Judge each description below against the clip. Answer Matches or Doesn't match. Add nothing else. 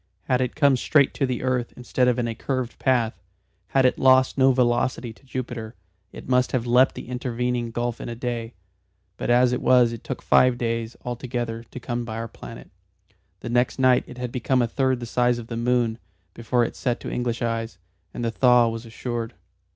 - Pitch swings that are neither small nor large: Doesn't match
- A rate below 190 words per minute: Doesn't match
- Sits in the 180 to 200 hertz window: Doesn't match